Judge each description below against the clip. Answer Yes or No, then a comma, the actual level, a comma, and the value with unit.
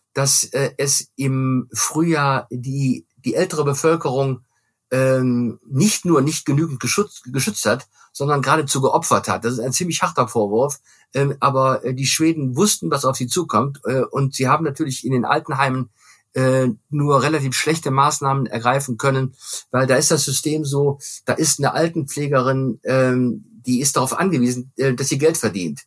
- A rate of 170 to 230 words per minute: No, average, 150 wpm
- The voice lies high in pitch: No, low, 135 Hz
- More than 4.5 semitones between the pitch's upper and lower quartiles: No, narrow, 2.5 semitones